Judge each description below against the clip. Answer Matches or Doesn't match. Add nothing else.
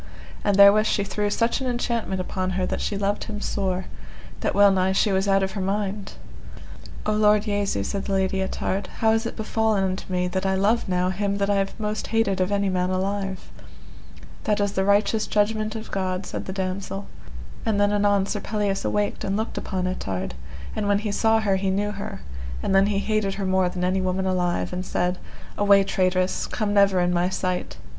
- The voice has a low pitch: Doesn't match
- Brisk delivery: Matches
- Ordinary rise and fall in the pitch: Doesn't match